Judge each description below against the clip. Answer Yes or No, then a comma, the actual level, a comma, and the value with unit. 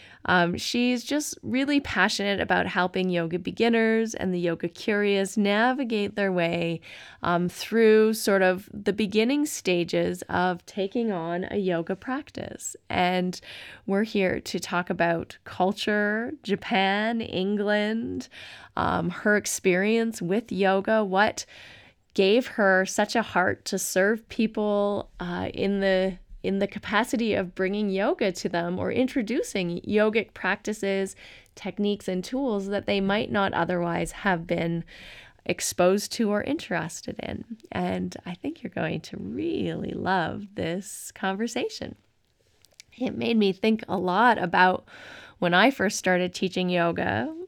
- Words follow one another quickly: No, slow, 135 wpm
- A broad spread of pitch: No, average, 3.3 semitones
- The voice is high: Yes, high, 200 Hz